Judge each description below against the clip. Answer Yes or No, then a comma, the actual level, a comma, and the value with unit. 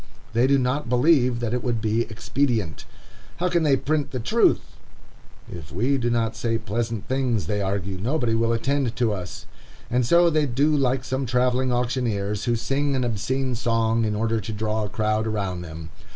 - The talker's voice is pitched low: Yes, low, 120 Hz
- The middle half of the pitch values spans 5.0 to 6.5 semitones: No, average, 3.3 semitones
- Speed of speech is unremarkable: Yes, average, 185 wpm